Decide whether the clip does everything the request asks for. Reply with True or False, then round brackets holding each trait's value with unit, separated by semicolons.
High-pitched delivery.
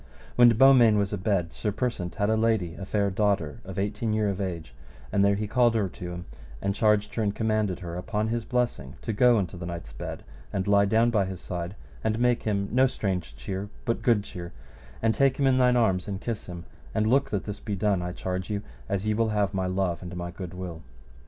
False (100 Hz)